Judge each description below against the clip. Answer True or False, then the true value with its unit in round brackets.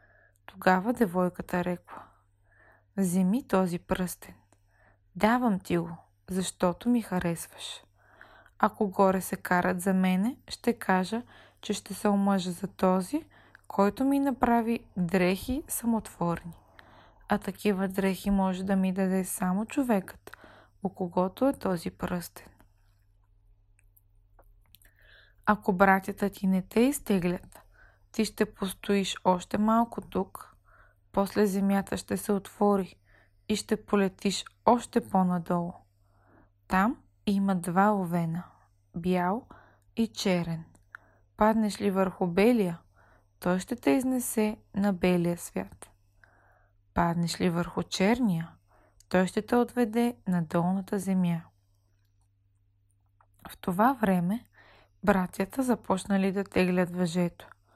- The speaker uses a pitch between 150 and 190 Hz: True (185 Hz)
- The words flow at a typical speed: False (110 wpm)